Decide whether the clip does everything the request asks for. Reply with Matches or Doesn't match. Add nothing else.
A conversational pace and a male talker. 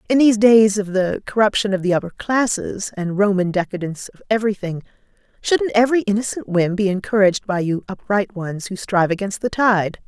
Doesn't match